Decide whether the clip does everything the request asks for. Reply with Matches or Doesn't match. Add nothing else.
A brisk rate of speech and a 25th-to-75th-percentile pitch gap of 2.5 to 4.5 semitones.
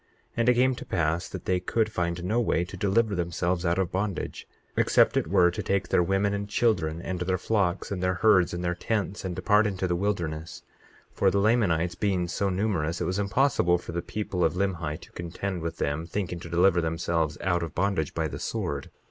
Matches